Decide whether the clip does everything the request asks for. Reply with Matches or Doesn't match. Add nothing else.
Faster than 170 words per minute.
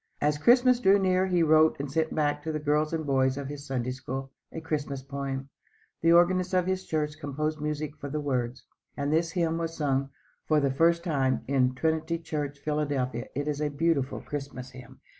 Matches